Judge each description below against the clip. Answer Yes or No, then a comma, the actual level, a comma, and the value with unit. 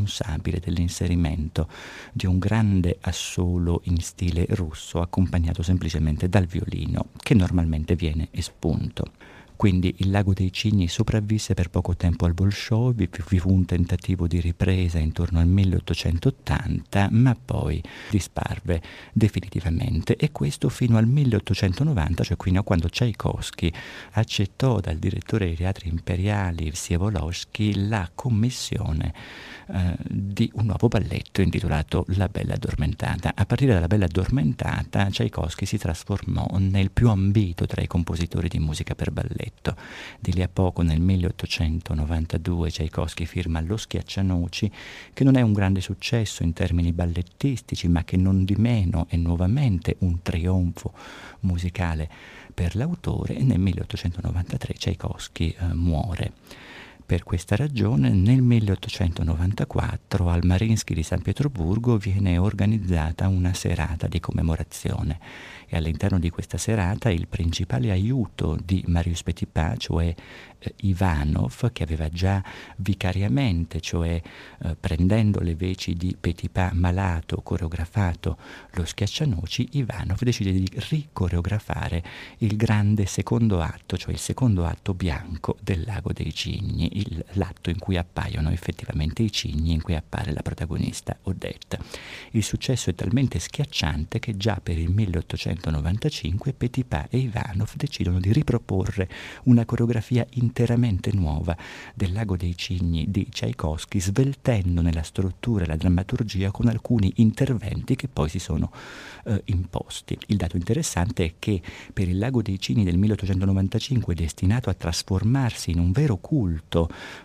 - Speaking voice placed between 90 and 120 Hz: Yes, very low, 95 Hz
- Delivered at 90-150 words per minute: Yes, average, 135 wpm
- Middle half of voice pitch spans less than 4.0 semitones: No, average, 4.3 semitones